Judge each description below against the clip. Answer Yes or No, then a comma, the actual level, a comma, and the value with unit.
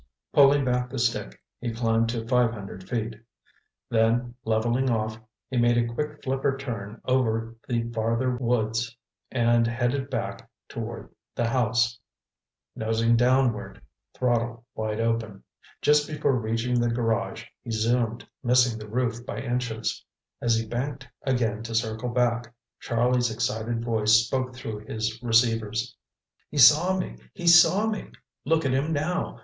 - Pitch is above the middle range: No, low, 120 Hz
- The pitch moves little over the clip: Yes, narrow, 2.0 semitones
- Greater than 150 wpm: No, average, 140 wpm